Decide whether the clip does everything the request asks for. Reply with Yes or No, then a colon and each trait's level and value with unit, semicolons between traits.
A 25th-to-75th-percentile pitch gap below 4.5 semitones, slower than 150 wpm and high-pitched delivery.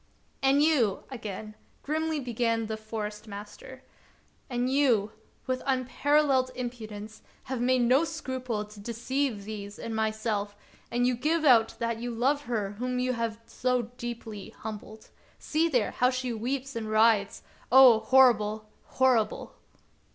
Yes: average, 3.2 semitones; average, 140 wpm; high, 240 Hz